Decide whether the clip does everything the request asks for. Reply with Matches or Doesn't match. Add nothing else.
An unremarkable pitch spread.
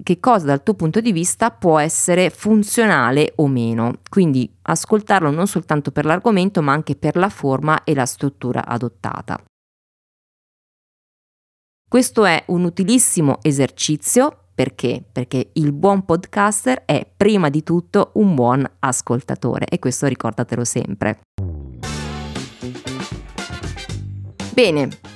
Doesn't match